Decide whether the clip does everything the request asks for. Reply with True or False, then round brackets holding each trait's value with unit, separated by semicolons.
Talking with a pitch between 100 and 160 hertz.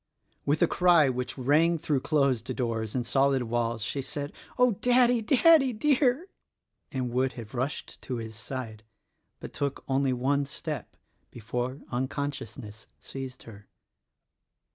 True (135 Hz)